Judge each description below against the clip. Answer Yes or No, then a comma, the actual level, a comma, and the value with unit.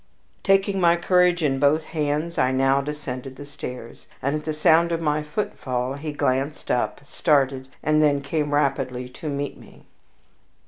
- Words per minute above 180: No, average, 165 wpm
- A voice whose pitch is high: No, medium, 145 Hz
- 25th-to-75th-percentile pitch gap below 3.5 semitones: Yes, average, 2.7 semitones